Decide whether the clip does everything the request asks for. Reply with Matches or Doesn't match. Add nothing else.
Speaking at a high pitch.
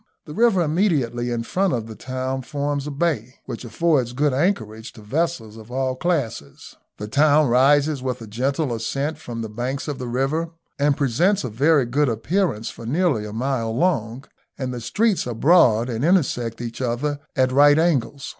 Doesn't match